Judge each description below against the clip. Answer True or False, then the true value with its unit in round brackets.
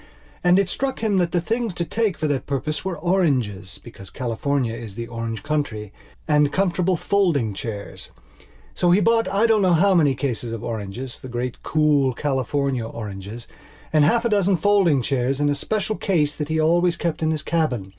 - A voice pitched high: False (150 Hz)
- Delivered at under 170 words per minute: False (180 wpm)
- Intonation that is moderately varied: False (7.0 semitones)